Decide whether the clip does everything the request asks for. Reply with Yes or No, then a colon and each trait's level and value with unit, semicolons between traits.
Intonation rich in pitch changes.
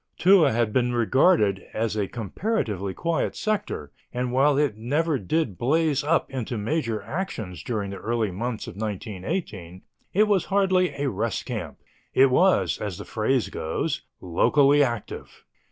Yes: wide, 7.1 semitones